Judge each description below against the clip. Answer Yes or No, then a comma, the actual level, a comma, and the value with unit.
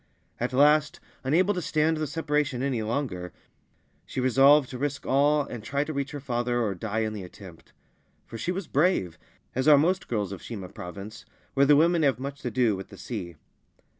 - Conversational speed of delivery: Yes, average, 195 wpm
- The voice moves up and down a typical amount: Yes, average, 4.9 semitones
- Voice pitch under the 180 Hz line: Yes, low, 135 Hz